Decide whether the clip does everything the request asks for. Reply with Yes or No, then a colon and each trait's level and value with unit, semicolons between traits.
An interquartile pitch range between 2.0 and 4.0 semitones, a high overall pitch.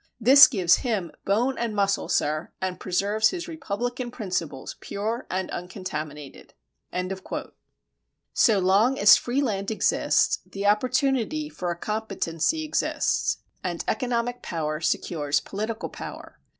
No: average, 5.3 semitones; high, 205 Hz